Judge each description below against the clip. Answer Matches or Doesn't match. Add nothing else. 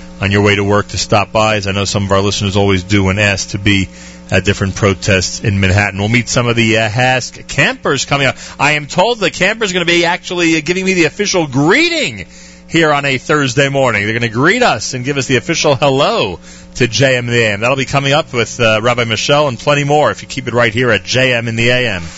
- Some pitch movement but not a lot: Doesn't match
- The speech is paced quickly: Matches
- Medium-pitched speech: Doesn't match